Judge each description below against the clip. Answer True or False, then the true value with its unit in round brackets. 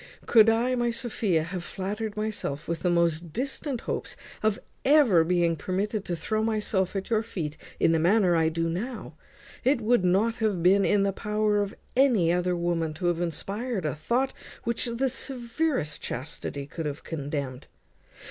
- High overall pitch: True (195 Hz)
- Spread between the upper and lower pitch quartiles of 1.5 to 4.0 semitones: False (5.3 semitones)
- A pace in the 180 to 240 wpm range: False (170 wpm)